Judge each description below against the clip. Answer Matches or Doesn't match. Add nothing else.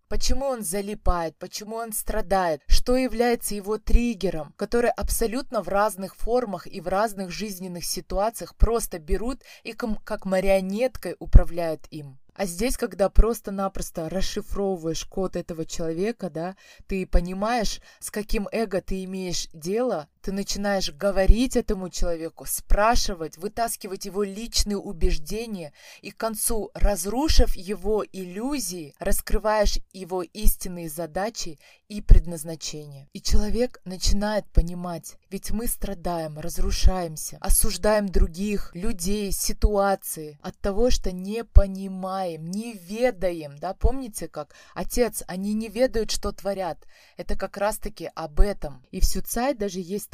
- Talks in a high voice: Matches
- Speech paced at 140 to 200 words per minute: Doesn't match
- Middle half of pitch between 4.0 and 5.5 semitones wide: Doesn't match